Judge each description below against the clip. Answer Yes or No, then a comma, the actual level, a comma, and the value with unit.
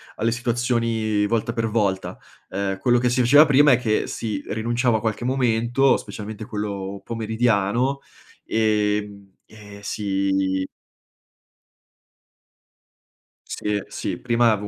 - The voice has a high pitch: No, low, 110 Hz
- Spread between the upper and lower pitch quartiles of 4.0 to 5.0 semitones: No, average, 2.7 semitones